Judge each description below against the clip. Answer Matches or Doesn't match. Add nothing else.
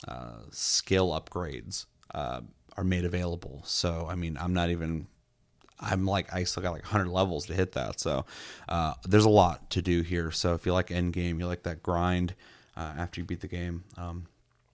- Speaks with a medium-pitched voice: Doesn't match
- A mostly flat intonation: Matches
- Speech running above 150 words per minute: Matches